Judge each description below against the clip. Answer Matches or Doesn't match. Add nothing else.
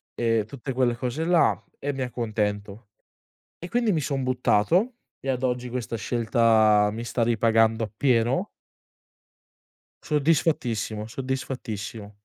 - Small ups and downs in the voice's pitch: Doesn't match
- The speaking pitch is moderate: Doesn't match